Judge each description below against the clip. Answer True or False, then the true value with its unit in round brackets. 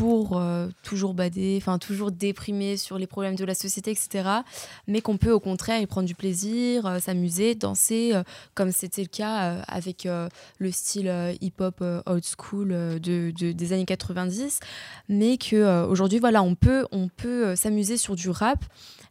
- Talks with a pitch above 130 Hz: True (190 Hz)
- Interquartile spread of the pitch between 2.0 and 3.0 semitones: True (2.7 semitones)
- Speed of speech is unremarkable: True (190 wpm)